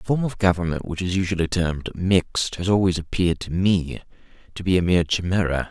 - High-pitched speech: No, very low, 90 Hz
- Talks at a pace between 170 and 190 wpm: No, average, 200 wpm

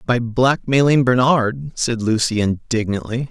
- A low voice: Yes, low, 120 Hz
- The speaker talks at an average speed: No, slow, 110 wpm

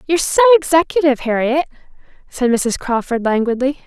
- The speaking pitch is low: No, very high, 275 Hz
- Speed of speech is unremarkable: No, slow, 125 wpm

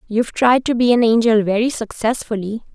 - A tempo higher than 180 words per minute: No, average, 175 wpm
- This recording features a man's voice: No, female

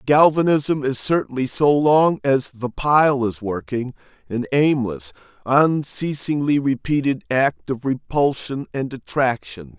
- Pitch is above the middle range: No, low, 135 Hz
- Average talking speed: No, slow, 115 wpm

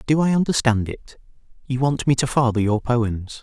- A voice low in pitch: Yes, low, 125 Hz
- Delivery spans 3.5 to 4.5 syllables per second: No, 5.0 syllables/s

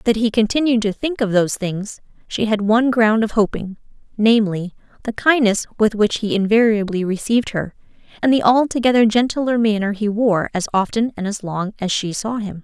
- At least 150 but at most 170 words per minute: No, average, 185 wpm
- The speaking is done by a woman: Yes, female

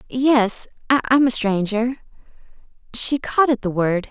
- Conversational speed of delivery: No, slow, 130 wpm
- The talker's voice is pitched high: Yes, high, 235 Hz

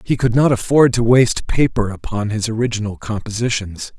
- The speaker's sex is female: No, male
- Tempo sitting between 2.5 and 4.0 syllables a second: No, 5.4 syllables/s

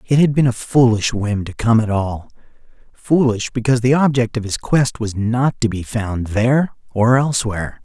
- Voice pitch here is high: No, low, 115 Hz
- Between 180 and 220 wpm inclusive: Yes, average, 185 wpm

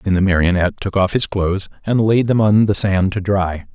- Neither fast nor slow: No, fast, 240 wpm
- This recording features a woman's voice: No, male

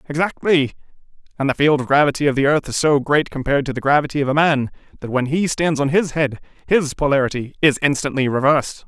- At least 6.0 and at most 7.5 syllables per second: Yes, 6.3 syllables/s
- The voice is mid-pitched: Yes, medium, 145 Hz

